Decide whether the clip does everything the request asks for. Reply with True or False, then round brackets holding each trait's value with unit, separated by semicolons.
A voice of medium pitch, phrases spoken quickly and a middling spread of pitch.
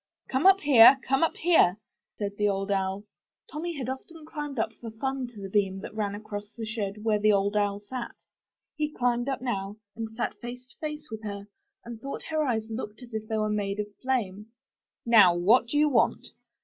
False (220 Hz; 210 wpm; 4.2 semitones)